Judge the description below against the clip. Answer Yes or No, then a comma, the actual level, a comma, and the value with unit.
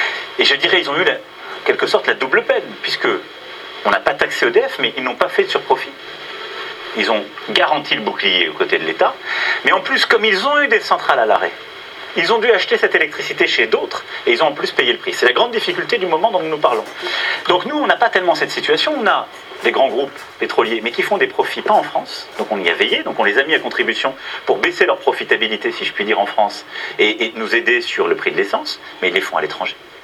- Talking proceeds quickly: Yes, fast, 260 wpm